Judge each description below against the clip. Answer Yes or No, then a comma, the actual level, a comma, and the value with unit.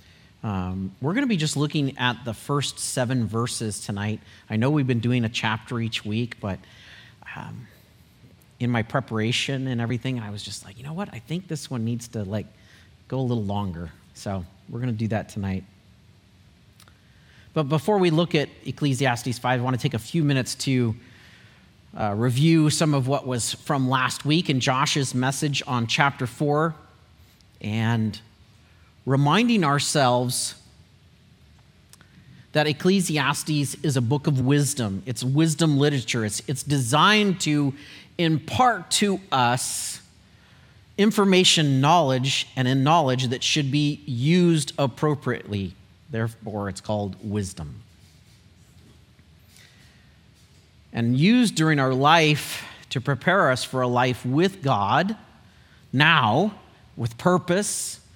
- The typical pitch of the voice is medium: No, low, 125 Hz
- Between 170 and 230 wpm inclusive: No, average, 140 wpm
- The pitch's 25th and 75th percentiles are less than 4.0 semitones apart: No, average, 5.2 semitones